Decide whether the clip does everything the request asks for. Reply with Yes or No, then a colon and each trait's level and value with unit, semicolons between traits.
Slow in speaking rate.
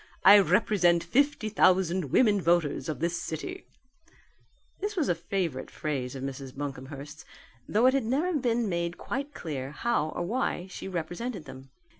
No: average, 160 wpm